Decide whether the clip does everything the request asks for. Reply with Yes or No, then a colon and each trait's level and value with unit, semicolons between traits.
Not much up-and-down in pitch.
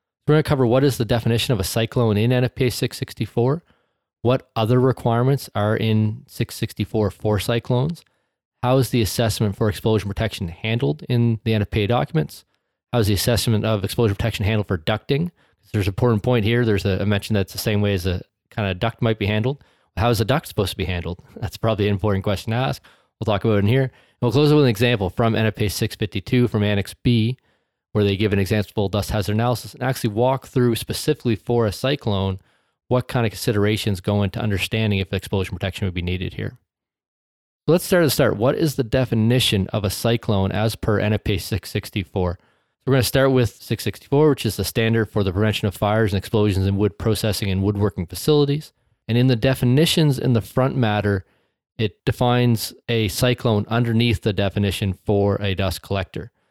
No: average, 3.3 semitones